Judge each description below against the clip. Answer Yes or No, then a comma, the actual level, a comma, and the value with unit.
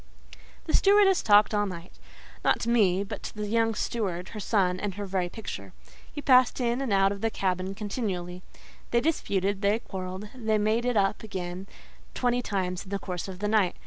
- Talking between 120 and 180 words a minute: No, average, 195 wpm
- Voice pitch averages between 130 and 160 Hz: No, high, 205 Hz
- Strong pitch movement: No, average, 3.3 semitones